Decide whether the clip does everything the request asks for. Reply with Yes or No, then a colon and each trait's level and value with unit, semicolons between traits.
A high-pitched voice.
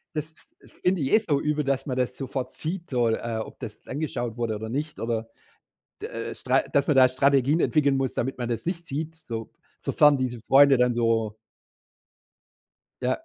No: low, 135 Hz